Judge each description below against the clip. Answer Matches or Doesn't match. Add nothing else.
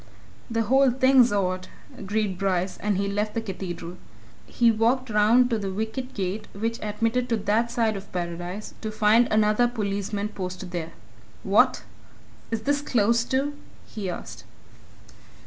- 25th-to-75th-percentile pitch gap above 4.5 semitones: Doesn't match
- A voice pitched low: Doesn't match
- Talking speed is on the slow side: Doesn't match